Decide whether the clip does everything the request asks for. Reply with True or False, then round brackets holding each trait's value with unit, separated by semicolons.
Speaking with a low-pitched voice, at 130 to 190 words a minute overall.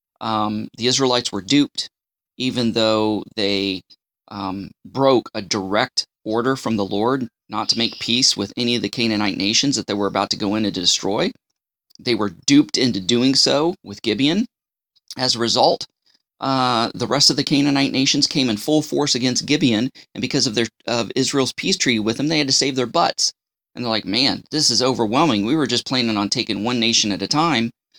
False (120 Hz; 200 wpm)